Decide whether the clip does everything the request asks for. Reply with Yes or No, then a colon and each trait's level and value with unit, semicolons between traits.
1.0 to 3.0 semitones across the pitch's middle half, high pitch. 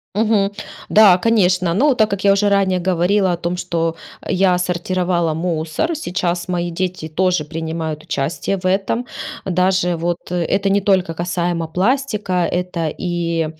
No: narrow, 2.5 semitones; medium, 180 Hz